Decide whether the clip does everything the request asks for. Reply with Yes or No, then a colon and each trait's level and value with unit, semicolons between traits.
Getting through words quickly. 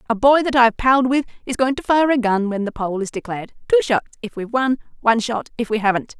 Yes: fast, 260 wpm